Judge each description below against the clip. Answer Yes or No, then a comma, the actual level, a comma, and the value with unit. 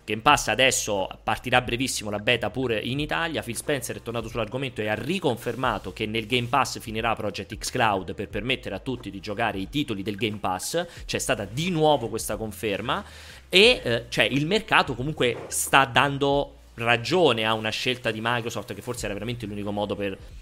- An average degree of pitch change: Yes, average, 3.6 semitones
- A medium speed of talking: No, fast, 190 wpm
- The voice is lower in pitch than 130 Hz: Yes, low, 115 Hz